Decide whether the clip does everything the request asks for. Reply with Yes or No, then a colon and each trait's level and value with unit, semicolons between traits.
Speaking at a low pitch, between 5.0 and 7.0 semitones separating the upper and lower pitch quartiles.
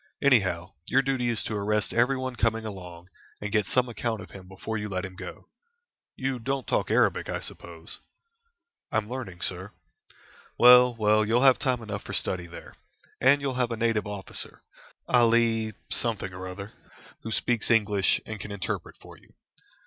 No: low, 110 Hz; average, 3.7 semitones